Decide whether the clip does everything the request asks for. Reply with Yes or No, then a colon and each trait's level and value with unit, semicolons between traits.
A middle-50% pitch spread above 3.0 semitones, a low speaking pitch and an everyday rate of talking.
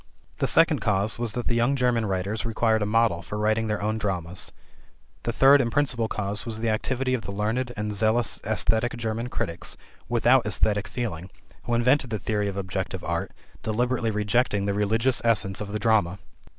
No: narrow, 2.6 semitones; low, 110 Hz; average, 185 wpm